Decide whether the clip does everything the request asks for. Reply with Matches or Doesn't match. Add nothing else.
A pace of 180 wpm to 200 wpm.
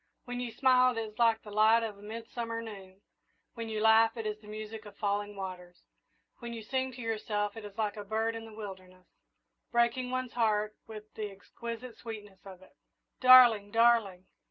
Matches